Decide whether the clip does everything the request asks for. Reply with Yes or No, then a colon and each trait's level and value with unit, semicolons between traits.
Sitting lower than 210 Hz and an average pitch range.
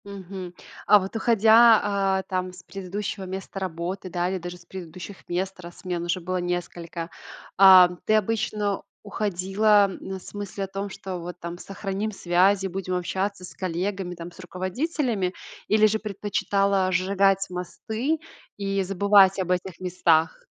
No: high, 190 Hz; narrow, 2.0 semitones